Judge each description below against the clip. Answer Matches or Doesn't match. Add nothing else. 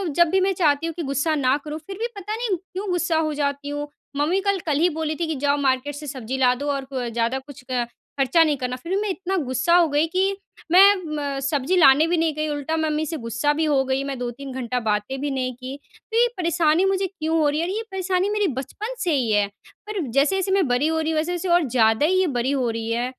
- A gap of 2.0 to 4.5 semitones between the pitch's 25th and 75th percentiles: Doesn't match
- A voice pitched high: Matches